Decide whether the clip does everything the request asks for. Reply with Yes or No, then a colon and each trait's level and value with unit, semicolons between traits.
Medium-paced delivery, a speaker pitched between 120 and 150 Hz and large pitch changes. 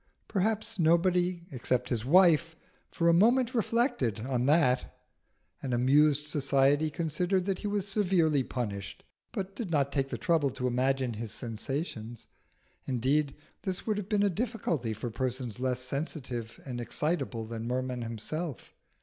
Yes: average, 145 wpm; medium, 140 Hz; wide, 6.2 semitones